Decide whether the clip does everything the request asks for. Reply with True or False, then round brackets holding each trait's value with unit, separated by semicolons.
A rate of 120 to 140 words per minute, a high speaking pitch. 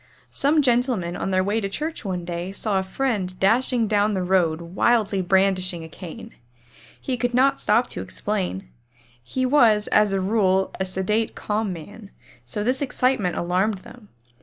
False (165 wpm; 200 Hz)